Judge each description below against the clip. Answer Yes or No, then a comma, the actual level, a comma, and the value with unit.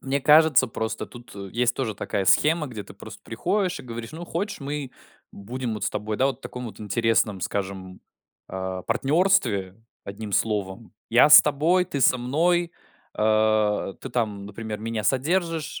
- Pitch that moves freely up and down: Yes, wide, 5.7 semitones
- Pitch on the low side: Yes, low, 115 Hz